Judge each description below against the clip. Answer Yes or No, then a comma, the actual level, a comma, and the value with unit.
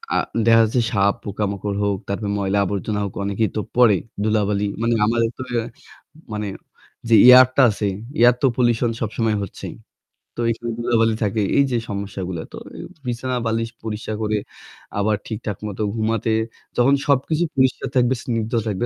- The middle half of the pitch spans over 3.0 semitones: No, narrow, 2.6 semitones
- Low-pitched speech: Yes, low, 110 Hz